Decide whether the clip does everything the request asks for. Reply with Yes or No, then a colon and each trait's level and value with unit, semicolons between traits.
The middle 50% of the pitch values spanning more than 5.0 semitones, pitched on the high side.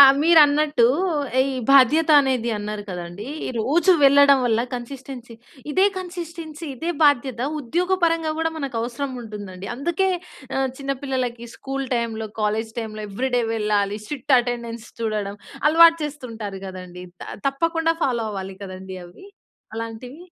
Yes: wide, 5.5 semitones; very high, 250 Hz